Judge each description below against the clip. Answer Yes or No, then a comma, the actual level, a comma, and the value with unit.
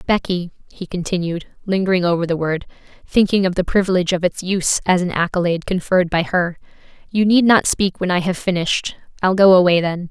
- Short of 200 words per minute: Yes, average, 190 wpm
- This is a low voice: No, medium, 180 Hz